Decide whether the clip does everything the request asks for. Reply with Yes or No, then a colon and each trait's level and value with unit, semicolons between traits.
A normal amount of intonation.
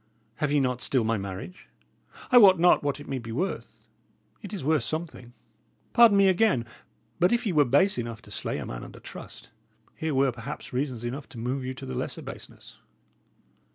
No: wide, 6.8 semitones